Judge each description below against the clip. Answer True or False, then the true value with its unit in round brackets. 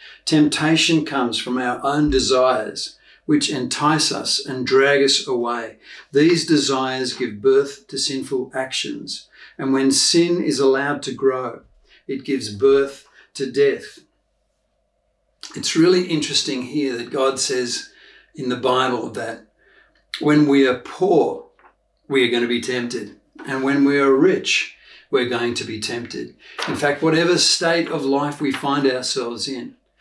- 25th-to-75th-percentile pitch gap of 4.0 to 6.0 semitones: False (3.4 semitones)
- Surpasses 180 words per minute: False (145 wpm)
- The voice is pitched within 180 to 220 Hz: False (140 Hz)